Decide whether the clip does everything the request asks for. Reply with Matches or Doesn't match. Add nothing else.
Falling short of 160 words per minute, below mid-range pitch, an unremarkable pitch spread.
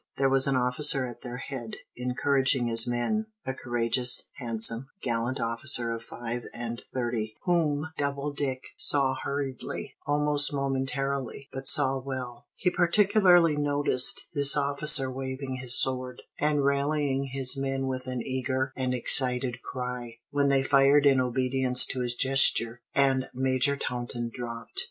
Doesn't match